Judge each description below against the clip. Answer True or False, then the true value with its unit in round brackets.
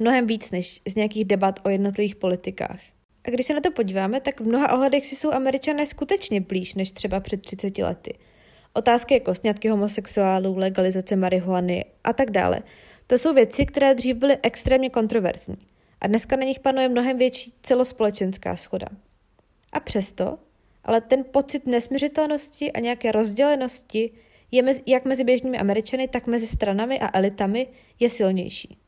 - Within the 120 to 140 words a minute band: False (160 wpm)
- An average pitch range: True (4.8 semitones)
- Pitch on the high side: True (230 Hz)